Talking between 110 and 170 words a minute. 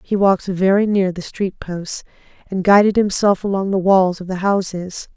No: average, 185 wpm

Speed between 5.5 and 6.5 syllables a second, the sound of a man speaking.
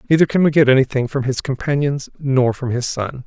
Yes: 5.8 syllables/s; male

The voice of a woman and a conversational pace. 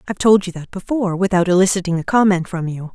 No: female; fast, 225 wpm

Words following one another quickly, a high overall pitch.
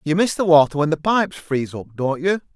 No: fast, 260 wpm; medium, 160 Hz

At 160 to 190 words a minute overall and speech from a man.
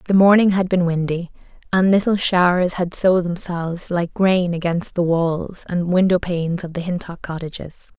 No: average, 175 wpm; female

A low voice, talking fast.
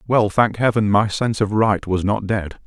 Yes: low, 105 Hz; fast, 225 wpm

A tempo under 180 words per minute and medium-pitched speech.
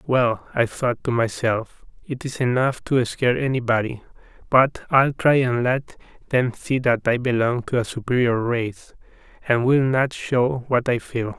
No: average, 170 wpm; low, 125 Hz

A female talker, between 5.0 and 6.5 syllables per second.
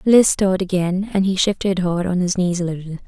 Yes: female; 5.7 syllables/s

